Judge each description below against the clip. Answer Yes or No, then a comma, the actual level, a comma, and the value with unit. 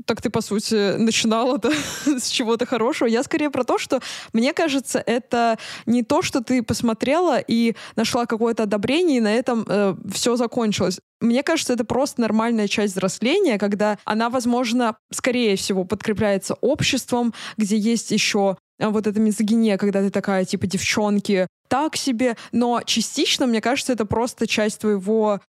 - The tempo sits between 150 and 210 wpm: Yes, fast, 160 wpm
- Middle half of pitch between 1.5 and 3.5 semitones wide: Yes, average, 2.9 semitones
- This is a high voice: Yes, high, 230 Hz